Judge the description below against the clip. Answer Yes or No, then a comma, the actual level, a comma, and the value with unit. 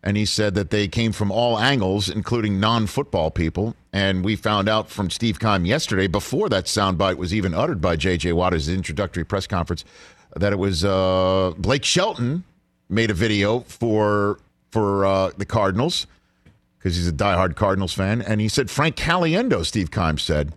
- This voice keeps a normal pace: Yes, average, 175 wpm